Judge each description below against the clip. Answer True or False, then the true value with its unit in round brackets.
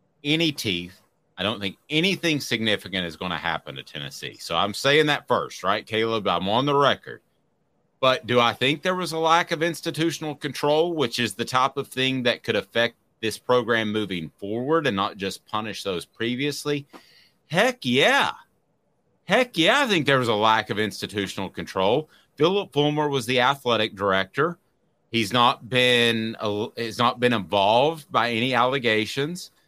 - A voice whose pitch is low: True (120 Hz)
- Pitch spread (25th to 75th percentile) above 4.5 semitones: True (5.5 semitones)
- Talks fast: False (170 wpm)